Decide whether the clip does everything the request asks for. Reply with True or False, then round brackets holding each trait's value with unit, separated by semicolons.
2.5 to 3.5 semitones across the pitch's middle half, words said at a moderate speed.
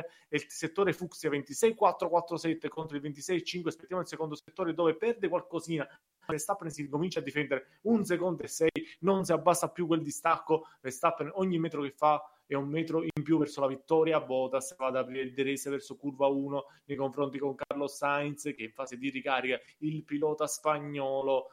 False (2.9 semitones; 185 wpm)